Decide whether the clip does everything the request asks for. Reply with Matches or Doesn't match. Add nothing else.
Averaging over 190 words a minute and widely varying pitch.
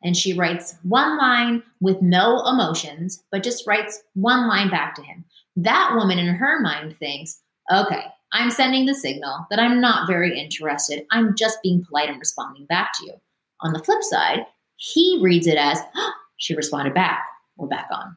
Doesn't match